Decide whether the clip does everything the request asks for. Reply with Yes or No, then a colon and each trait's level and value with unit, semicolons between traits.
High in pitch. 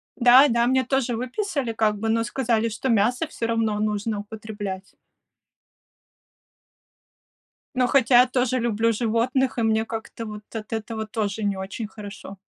Yes: high, 225 Hz